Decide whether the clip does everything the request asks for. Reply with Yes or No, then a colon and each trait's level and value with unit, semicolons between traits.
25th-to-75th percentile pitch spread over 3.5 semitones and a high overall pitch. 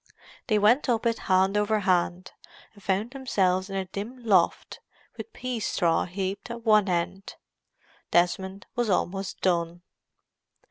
No: average, 3.2 semitones; high, 195 Hz